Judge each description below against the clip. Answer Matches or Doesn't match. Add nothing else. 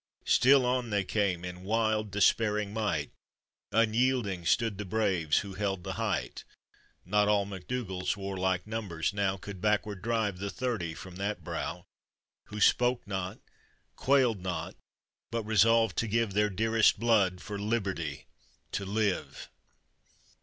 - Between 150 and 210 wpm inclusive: Doesn't match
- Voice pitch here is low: Matches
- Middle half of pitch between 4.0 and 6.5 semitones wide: Doesn't match